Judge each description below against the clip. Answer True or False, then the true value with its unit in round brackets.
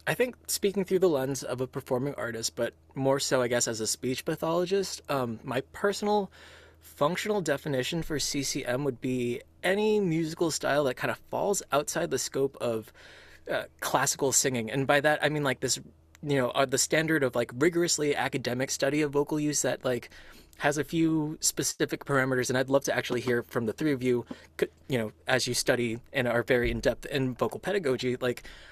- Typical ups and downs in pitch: True (3.6 semitones)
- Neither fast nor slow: True (190 wpm)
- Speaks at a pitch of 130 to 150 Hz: True (135 Hz)